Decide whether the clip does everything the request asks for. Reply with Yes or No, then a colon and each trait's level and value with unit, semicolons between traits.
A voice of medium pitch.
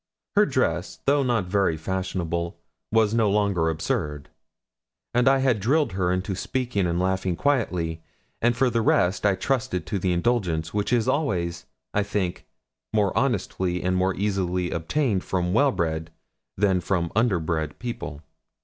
No: very low, 95 Hz